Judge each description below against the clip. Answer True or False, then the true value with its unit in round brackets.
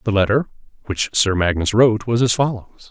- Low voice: True (110 Hz)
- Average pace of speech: True (185 wpm)